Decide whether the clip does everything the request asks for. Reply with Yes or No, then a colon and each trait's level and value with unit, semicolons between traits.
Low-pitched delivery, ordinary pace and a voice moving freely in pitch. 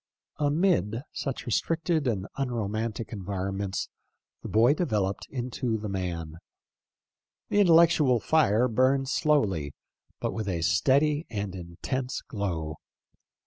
No: low, 115 Hz; slow, 115 wpm; wide, 6.3 semitones